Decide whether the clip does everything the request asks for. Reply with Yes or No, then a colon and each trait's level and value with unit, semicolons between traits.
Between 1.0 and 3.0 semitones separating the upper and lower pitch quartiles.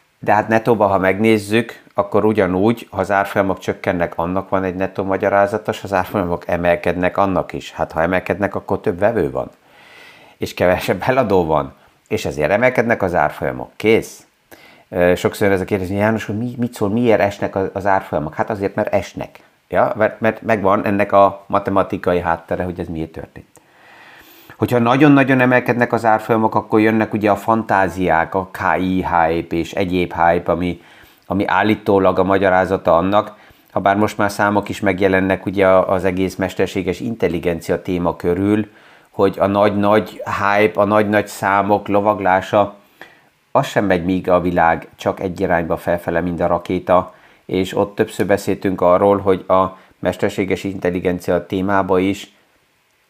Yes: narrow, 2.5 semitones